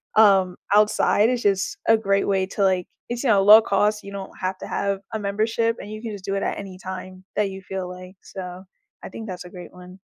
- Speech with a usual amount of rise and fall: No, narrow, 2.1 semitones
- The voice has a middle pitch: No, high, 195 Hz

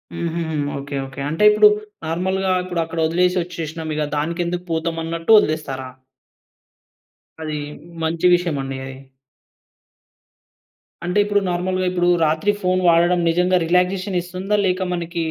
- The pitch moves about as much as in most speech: No, narrow, 2.2 semitones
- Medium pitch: Yes, medium, 170 Hz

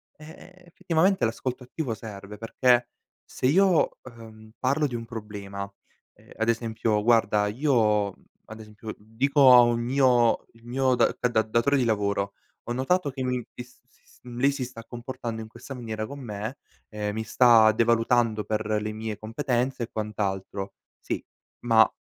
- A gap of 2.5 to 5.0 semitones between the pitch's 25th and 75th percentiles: Yes, average, 2.8 semitones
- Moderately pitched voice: No, low, 115 Hz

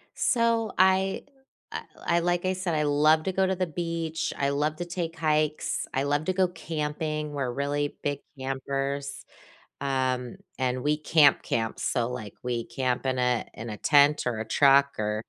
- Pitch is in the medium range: Yes, medium, 145 Hz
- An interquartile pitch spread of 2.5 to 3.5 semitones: No, average, 4.1 semitones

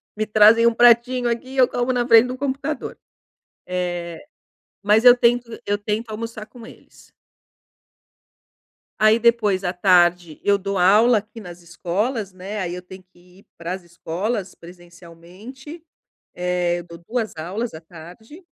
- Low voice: No, high, 205 Hz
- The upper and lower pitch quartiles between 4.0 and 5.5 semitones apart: Yes, average, 4.8 semitones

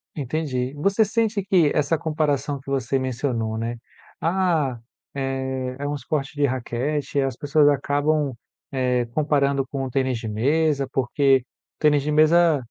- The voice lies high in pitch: No, medium, 140 Hz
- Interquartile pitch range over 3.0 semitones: No, average, 2.7 semitones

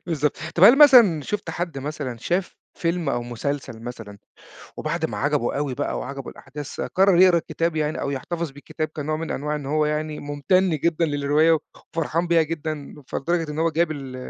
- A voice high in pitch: No, medium, 155 Hz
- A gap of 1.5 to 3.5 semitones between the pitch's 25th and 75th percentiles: Yes, average, 3.1 semitones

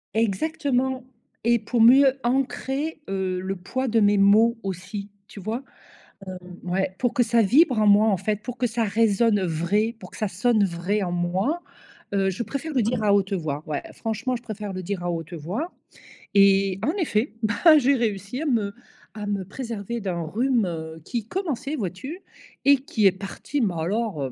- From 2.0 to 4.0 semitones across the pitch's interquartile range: No, average, 4.4 semitones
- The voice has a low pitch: No, high, 210 Hz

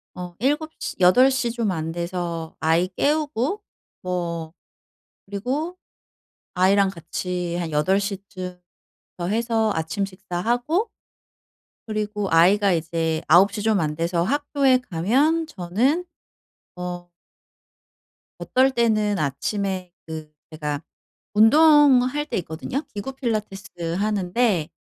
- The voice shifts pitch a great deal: Yes, wide, 6.1 semitones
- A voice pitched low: No, high, 195 Hz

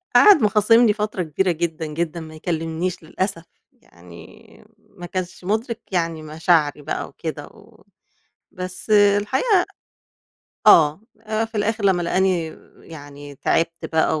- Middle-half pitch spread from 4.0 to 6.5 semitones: Yes, average, 4.6 semitones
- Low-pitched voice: No, medium, 175 Hz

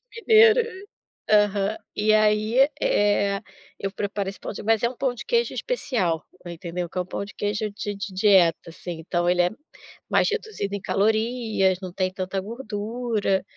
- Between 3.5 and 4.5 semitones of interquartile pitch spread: No, average, 3.1 semitones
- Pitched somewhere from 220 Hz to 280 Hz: No, high, 205 Hz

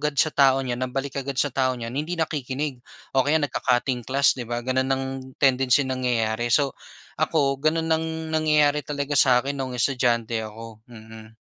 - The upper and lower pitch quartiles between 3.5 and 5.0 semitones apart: No, average, 2.8 semitones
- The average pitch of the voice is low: Yes, low, 130 Hz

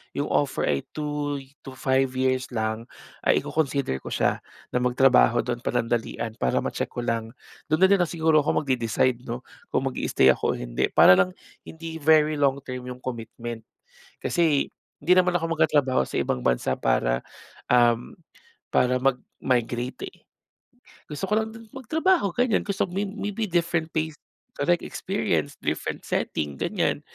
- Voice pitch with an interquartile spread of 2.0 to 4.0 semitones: No, wide, 5.4 semitones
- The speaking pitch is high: No, low, 135 Hz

